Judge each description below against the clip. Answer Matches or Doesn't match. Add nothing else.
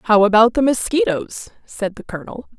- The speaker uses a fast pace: Doesn't match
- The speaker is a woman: Matches